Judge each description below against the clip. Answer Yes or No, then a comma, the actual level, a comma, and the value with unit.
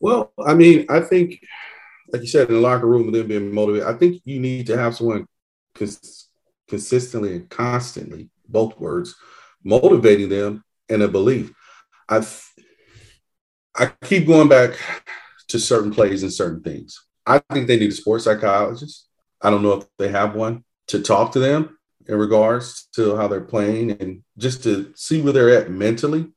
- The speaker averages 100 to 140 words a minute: No, average, 175 wpm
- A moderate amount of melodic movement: Yes, average, 4.3 semitones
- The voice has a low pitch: Yes, low, 115 Hz